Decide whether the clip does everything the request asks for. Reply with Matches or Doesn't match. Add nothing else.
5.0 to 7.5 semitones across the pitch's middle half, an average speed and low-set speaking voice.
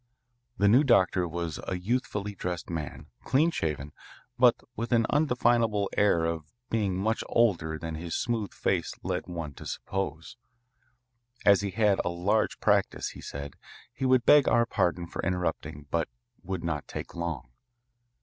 Matches